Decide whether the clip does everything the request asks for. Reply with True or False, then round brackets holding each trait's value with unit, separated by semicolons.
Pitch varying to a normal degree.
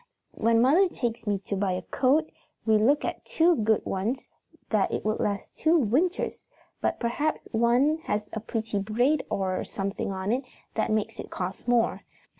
True (4.8 semitones)